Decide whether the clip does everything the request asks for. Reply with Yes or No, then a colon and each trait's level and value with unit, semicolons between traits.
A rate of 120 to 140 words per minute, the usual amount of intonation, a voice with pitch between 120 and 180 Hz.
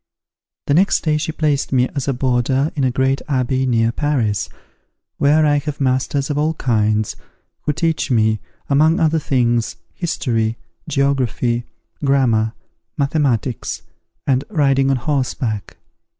Yes: slow, 135 wpm; average, 3.4 semitones; low, 135 Hz